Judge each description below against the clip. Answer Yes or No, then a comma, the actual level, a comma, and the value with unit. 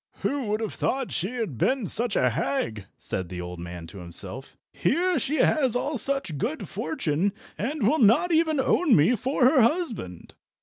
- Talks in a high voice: Yes, high, 225 Hz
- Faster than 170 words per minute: Yes, average, 180 wpm